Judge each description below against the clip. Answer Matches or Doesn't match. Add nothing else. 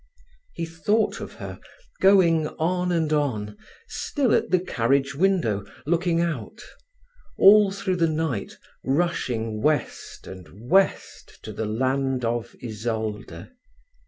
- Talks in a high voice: Doesn't match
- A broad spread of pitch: Matches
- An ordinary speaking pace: Doesn't match